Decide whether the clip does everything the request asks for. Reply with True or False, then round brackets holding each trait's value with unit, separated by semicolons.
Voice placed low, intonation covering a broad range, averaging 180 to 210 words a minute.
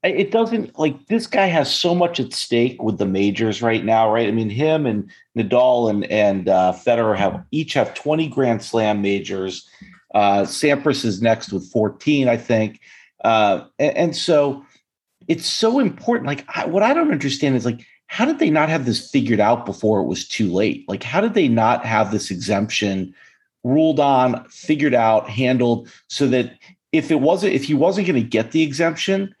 True (125 Hz; 6.6 semitones; 190 wpm)